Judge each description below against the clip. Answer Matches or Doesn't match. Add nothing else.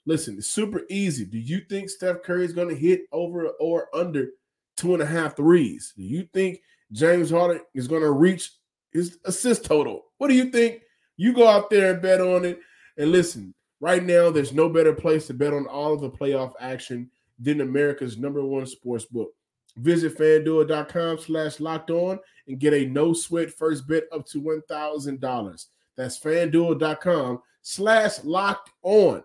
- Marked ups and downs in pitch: Doesn't match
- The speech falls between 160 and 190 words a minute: Matches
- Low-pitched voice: Doesn't match